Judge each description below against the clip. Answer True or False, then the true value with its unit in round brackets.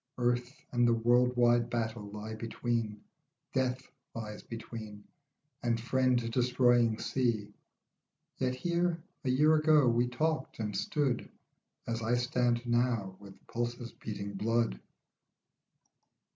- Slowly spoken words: True (115 wpm)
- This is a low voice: True (120 Hz)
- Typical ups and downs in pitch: False (2.0 semitones)